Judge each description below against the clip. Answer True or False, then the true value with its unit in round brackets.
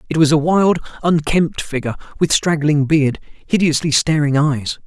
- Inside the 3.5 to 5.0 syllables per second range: True (4.7 syllables/s)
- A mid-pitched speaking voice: True (155 Hz)